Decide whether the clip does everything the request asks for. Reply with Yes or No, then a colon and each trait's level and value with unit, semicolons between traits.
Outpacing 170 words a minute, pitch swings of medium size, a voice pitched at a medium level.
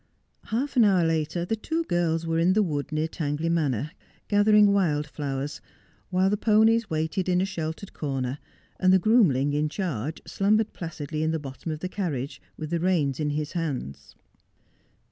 Yes: average, 180 wpm; average, 4.6 semitones; medium, 165 Hz